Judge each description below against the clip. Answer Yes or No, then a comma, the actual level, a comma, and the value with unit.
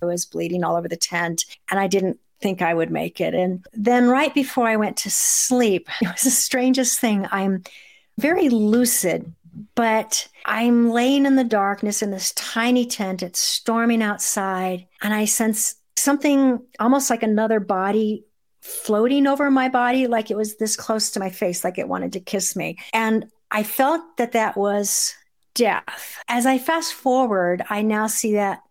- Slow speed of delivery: No, average, 180 wpm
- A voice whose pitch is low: No, high, 220 Hz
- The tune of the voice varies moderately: Yes, average, 4.0 semitones